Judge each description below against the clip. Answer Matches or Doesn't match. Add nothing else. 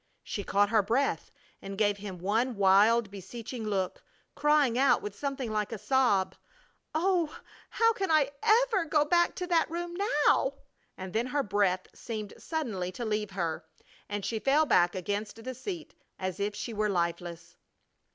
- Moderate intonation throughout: Doesn't match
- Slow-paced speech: Doesn't match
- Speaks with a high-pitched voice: Matches